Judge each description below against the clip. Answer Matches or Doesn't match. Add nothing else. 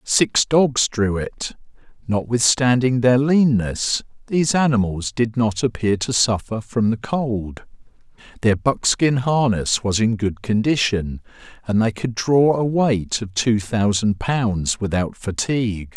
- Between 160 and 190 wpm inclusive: Doesn't match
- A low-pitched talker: Matches